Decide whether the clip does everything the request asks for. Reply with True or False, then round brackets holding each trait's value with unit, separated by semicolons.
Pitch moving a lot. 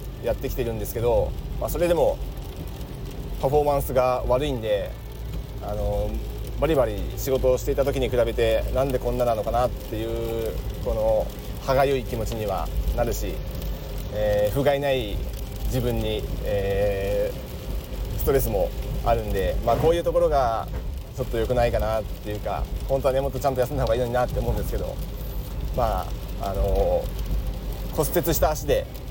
False (4.3 semitones)